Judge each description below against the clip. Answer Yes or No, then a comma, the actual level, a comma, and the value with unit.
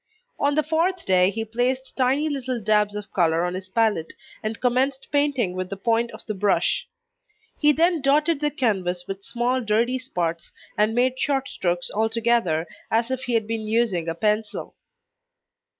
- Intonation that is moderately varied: Yes, average, 5.0 semitones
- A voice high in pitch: Yes, high, 230 Hz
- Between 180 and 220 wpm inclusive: No, average, 170 wpm